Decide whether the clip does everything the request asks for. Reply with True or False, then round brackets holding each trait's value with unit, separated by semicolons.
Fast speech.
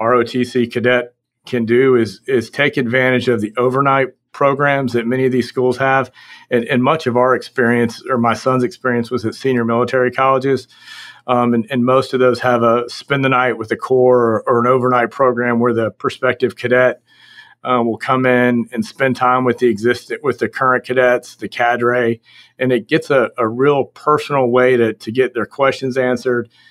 False (195 wpm)